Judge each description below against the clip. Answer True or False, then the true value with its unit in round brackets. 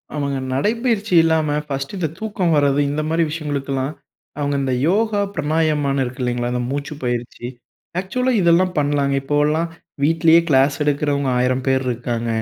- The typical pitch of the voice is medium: True (145 Hz)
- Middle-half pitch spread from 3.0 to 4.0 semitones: True (3.5 semitones)